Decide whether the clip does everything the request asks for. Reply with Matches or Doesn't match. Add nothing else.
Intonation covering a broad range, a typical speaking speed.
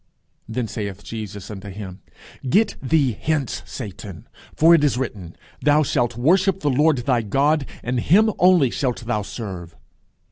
Matches